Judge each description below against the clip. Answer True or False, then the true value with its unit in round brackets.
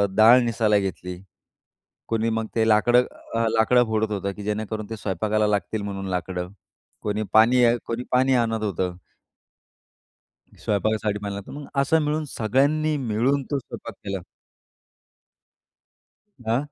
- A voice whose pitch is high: False (110 Hz)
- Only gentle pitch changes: False (3.0 semitones)